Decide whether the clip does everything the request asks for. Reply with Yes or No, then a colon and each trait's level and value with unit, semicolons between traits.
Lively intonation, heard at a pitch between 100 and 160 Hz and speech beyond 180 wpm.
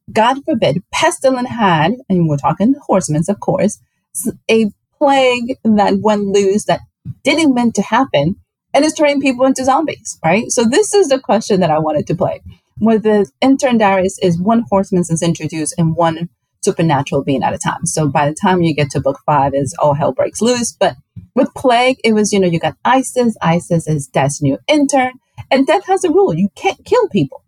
No: wide, 7.4 semitones; high, 205 Hz; average, 200 wpm